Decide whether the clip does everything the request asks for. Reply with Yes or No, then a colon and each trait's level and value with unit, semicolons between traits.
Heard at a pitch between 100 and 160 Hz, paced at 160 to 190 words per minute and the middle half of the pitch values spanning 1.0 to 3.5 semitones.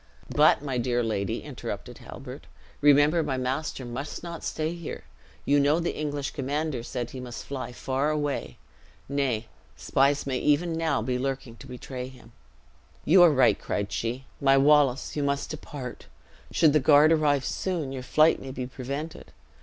Yes: medium, 140 Hz; average, 165 wpm; average, 3.0 semitones